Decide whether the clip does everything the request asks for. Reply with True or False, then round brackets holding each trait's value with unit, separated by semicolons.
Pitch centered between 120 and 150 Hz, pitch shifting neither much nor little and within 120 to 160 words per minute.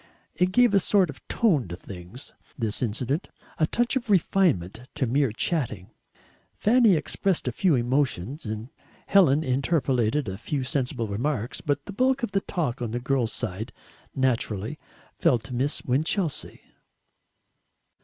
False (135 Hz; 6.9 semitones; 145 wpm)